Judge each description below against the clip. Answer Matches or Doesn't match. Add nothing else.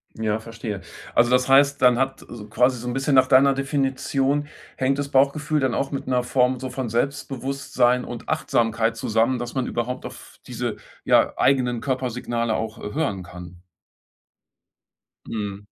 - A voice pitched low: Matches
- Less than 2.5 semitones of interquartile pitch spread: Doesn't match